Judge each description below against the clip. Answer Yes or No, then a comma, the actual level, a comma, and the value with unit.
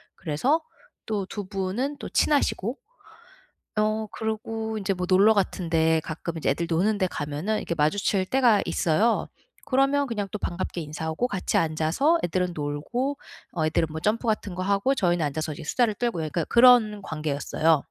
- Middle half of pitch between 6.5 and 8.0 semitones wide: No, wide, 5.5 semitones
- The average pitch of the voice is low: No, high, 195 Hz